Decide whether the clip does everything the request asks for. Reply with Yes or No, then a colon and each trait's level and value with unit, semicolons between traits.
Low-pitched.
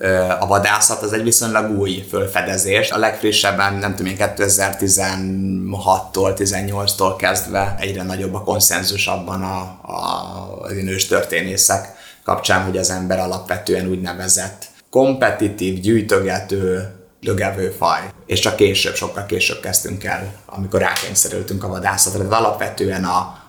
Yes: very low, 95 Hz